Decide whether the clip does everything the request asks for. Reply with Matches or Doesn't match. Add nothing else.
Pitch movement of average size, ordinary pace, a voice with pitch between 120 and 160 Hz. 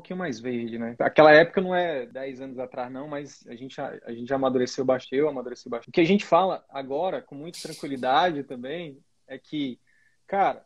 Doesn't match